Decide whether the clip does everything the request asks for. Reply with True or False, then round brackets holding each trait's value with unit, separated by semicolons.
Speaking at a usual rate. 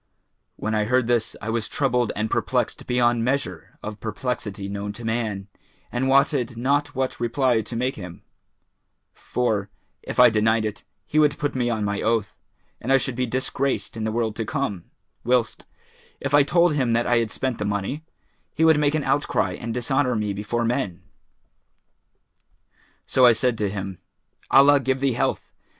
True (175 wpm)